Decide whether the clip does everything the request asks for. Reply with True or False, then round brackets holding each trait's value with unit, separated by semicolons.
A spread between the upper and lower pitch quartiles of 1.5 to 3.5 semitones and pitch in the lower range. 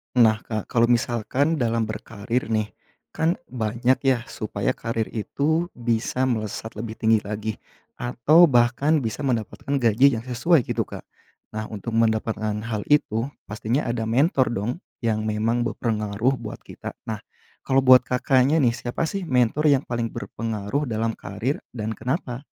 True (2.9 semitones; 115 Hz)